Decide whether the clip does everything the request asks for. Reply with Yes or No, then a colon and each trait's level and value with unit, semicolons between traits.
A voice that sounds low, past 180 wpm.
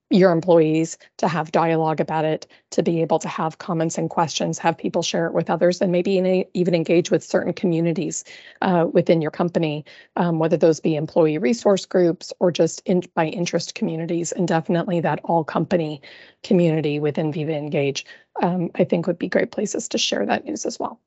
No: medium, 170 Hz; average, 195 wpm